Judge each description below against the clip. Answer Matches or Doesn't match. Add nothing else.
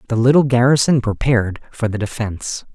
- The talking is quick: Doesn't match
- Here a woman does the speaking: Doesn't match